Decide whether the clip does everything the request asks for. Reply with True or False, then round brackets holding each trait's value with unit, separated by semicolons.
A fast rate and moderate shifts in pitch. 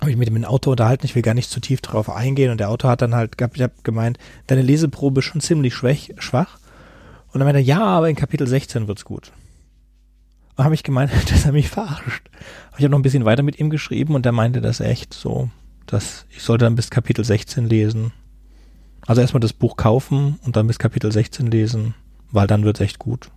True (230 wpm; 3.8 semitones)